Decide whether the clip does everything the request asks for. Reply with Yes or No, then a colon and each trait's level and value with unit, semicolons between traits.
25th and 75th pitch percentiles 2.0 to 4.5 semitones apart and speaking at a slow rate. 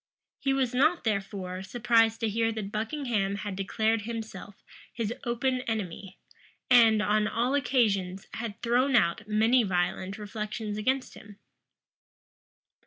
Yes: average, 2.9 semitones; slow, 125 wpm